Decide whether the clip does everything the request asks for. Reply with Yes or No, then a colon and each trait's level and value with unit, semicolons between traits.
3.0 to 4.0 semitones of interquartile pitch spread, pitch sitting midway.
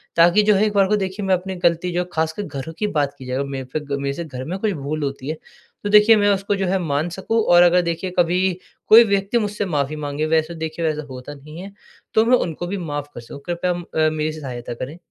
No: average, 4.6 semitones; medium, 170 Hz